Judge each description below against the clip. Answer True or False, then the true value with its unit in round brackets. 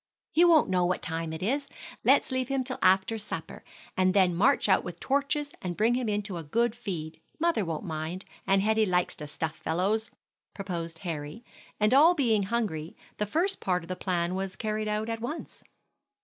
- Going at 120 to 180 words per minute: False (195 wpm)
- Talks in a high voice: True (200 Hz)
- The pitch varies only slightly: False (5.2 semitones)